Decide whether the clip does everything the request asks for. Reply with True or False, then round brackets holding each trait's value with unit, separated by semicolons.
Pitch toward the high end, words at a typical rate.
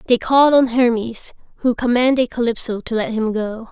True (235 Hz; 180 wpm)